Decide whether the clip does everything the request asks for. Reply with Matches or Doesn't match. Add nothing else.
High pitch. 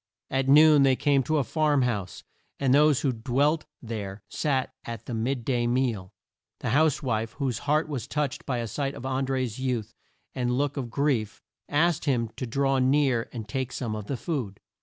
Doesn't match